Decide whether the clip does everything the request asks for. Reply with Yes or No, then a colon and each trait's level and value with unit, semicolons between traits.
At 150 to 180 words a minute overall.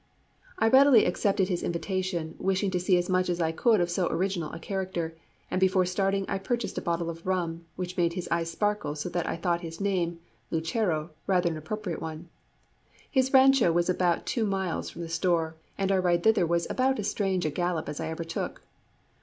No: fast, 205 wpm